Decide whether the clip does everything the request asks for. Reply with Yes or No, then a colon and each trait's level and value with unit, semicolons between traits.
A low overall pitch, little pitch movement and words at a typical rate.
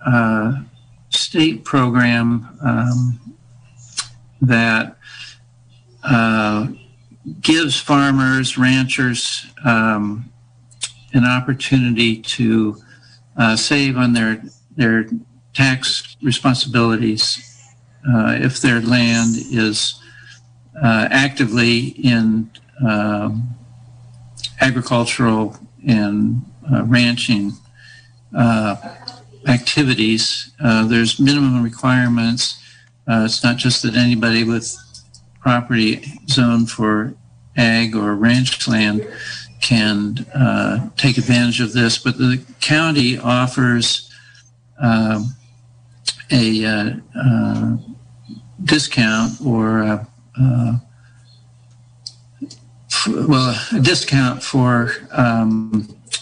No: low, 120 Hz; narrow, 1.6 semitones; slow, 85 wpm